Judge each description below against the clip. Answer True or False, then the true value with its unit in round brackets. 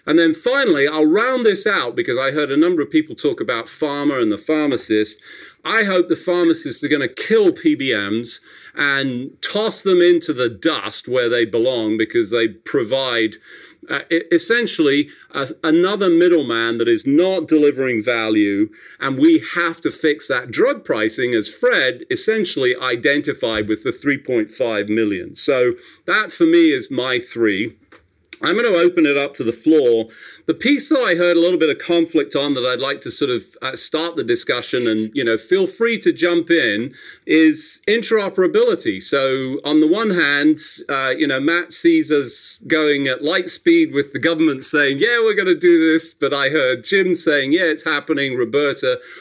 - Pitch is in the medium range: True (165 Hz)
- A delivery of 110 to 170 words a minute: False (180 wpm)